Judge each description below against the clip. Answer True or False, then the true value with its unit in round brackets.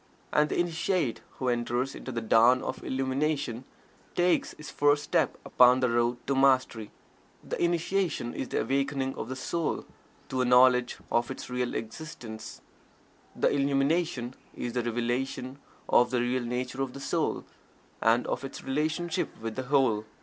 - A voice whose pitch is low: True (130 Hz)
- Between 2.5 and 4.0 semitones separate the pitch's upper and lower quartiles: True (2.8 semitones)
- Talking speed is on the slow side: False (155 wpm)